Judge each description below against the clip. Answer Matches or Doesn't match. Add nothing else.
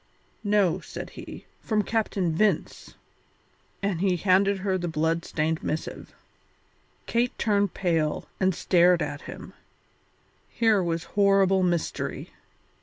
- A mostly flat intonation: Doesn't match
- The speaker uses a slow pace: Matches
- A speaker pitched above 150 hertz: Matches